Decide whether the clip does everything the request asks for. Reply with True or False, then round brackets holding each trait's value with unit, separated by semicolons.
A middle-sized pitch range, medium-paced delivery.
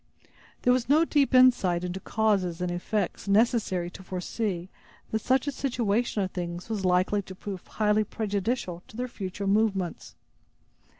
True (4.2 semitones; 155 wpm)